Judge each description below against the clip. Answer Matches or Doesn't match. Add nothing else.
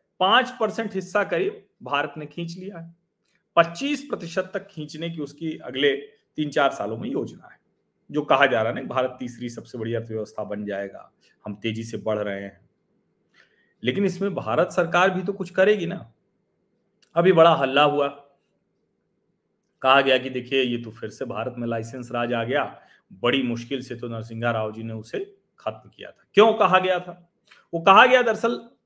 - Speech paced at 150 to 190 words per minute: Matches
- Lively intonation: Matches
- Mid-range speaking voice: Matches